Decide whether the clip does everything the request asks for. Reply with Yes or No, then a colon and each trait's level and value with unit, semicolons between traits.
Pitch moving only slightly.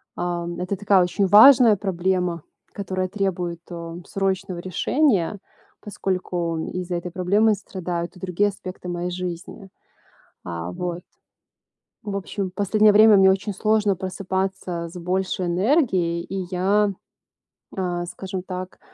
Yes: narrow, 2.2 semitones